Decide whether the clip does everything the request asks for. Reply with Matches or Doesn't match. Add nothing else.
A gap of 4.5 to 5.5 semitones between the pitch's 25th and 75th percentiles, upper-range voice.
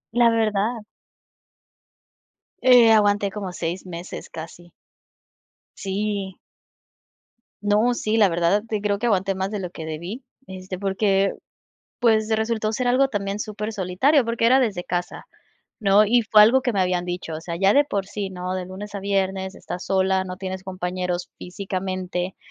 Doesn't match